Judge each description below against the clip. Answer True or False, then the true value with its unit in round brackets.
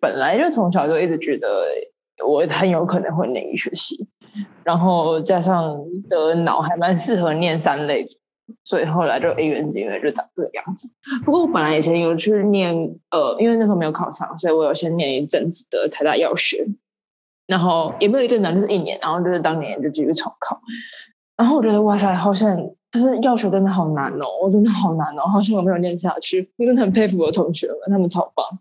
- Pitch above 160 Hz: True (190 Hz)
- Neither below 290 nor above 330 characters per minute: True (320 characters per minute)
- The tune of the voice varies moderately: True (4.3 semitones)